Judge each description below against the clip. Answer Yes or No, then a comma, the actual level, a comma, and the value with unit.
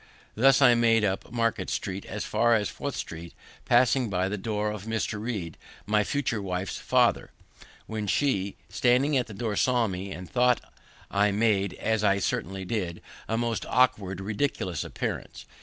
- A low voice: Yes, low, 105 Hz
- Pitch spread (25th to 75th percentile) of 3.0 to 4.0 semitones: Yes, average, 3.5 semitones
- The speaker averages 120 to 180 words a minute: Yes, average, 165 wpm